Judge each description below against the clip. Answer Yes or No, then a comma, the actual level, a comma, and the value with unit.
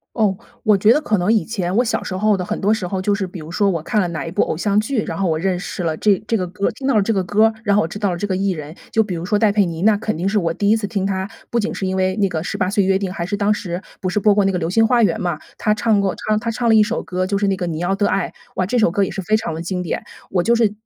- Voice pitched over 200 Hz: No, high, 195 Hz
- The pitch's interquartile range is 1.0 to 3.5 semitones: Yes, average, 2.8 semitones